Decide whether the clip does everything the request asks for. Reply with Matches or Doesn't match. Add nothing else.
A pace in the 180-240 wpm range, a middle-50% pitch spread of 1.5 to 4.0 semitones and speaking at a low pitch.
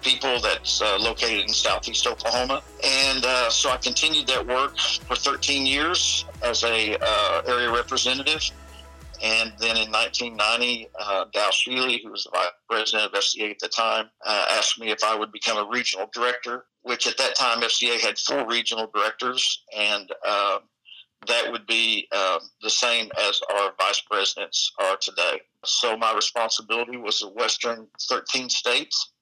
Doesn't match